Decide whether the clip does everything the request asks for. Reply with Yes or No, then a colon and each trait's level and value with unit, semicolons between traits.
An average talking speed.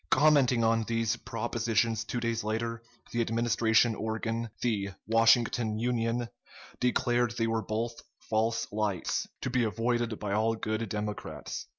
No: slow, 130 wpm